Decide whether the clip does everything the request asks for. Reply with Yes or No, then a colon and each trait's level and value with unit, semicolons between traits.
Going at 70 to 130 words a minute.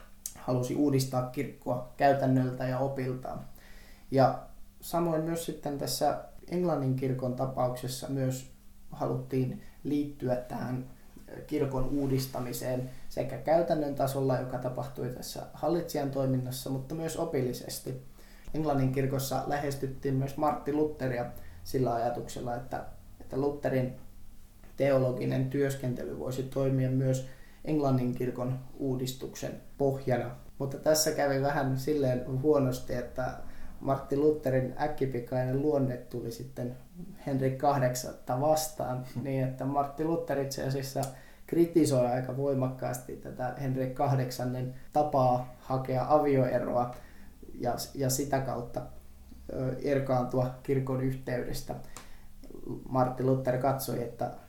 Yes: average, 100 wpm